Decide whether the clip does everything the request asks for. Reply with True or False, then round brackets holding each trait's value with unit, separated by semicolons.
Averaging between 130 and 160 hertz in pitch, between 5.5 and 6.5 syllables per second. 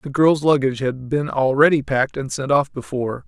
True (140 Hz; 5.6 syllables/s)